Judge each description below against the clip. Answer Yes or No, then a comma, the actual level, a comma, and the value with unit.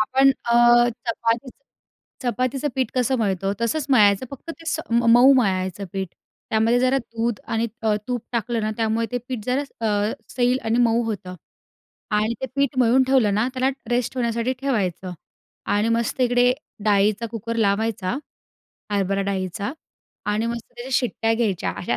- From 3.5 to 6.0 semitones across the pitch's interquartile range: No, average, 3.1 semitones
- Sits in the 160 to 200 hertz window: No, high, 230 Hz